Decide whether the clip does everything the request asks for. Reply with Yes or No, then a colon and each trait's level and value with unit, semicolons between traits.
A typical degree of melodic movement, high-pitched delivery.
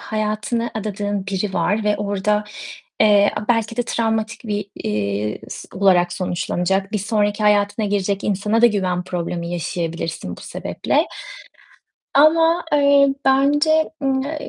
Yes: average, 3.4 semitones; high, 210 Hz